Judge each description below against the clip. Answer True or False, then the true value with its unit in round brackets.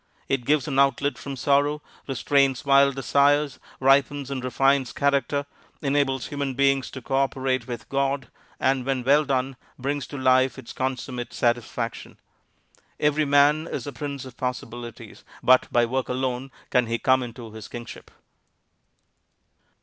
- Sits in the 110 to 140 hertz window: True (135 Hz)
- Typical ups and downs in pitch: False (1.9 semitones)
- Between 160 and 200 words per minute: False (140 wpm)